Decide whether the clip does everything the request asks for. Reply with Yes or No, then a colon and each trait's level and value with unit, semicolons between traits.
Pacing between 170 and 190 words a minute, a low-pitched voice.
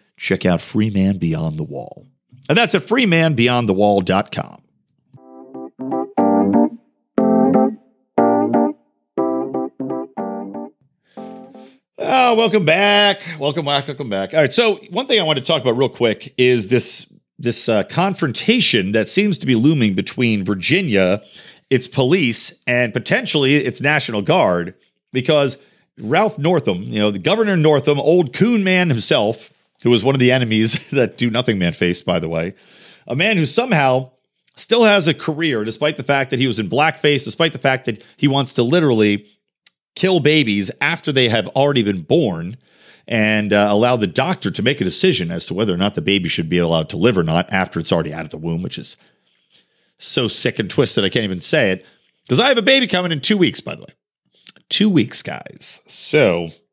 Yes: average, 175 wpm; low, 130 Hz